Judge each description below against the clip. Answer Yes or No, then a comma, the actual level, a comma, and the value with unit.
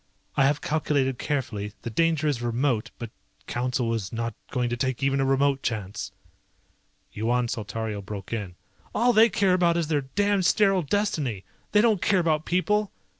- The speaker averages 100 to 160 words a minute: No, average, 170 wpm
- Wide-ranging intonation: Yes, wide, 6.8 semitones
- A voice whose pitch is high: No, low, 135 Hz